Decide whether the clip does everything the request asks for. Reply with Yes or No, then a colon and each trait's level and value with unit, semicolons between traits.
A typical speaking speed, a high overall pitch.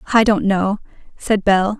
Yes: average, 165 wpm; high, 205 Hz